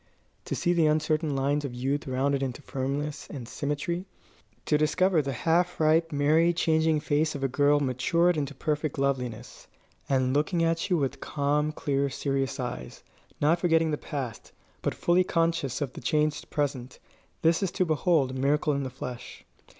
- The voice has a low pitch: No, medium, 145 Hz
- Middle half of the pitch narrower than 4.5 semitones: Yes, average, 2.9 semitones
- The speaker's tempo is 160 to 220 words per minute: Yes, average, 170 wpm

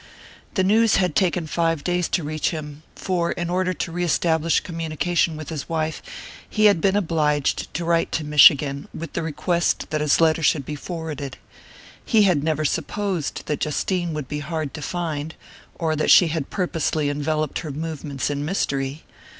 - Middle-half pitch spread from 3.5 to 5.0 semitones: No, average, 2.7 semitones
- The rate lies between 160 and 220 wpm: Yes, average, 175 wpm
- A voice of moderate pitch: Yes, medium, 160 Hz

